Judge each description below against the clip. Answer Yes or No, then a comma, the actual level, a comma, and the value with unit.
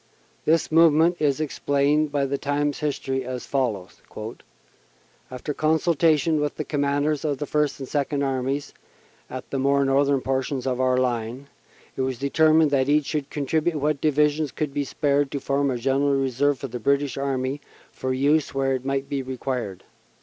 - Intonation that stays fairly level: Yes, narrow, 2.0 semitones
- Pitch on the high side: No, medium, 140 Hz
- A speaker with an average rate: Yes, average, 170 wpm